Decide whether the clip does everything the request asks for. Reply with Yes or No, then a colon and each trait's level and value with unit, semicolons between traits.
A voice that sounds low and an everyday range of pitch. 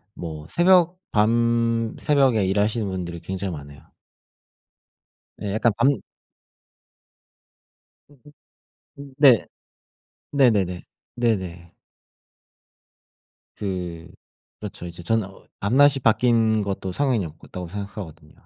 Yes: low, 105 Hz; average, 4.7 semitones